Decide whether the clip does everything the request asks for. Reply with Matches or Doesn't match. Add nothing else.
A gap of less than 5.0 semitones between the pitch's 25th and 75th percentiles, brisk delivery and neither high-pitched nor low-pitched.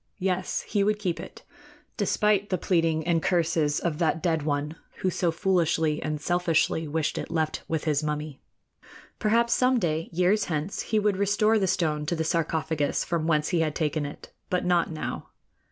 Doesn't match